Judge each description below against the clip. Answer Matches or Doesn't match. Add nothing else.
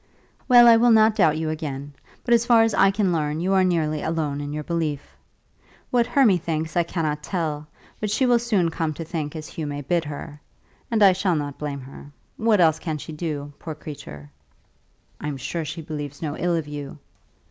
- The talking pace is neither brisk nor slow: Doesn't match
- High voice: Doesn't match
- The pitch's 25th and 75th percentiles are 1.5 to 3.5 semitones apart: Doesn't match